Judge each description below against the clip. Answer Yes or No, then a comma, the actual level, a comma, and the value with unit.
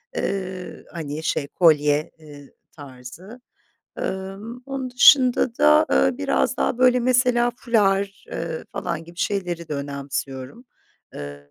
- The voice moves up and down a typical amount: No, wide, 8.5 semitones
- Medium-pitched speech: Yes, medium, 170 Hz